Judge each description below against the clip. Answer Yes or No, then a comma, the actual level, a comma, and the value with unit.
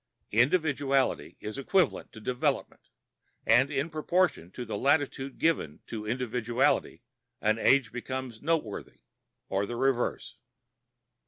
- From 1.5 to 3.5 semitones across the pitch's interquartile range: No, average, 4.0 semitones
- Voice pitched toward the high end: No, low, 130 Hz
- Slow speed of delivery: Yes, slow, 110 wpm